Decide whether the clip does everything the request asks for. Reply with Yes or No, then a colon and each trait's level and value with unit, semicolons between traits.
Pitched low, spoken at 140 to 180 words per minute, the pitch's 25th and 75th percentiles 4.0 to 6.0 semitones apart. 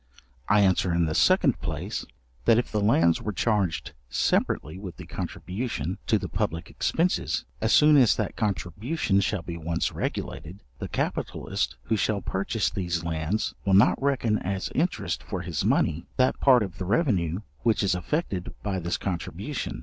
Yes: very low, 95 Hz; average, 165 wpm; average, 4.5 semitones